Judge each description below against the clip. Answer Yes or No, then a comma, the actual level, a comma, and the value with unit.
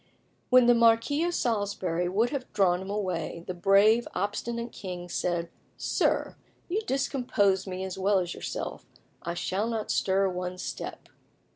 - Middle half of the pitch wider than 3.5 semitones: Yes, average, 4.3 semitones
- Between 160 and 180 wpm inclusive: No, average, 150 wpm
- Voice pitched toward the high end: Yes, high, 195 Hz